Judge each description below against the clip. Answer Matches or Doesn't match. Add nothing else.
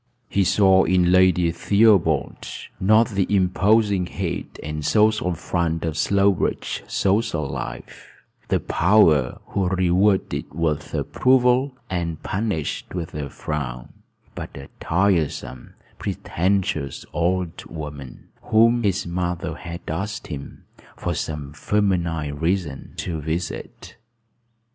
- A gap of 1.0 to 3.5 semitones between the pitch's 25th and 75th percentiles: Doesn't match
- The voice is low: Matches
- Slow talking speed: Matches